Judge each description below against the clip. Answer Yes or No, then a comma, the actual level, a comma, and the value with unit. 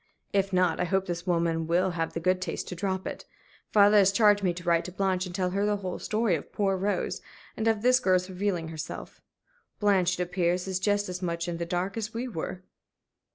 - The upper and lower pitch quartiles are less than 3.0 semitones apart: Yes, narrow, 2.4 semitones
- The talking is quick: Yes, fast, 225 wpm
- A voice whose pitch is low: No, medium, 185 Hz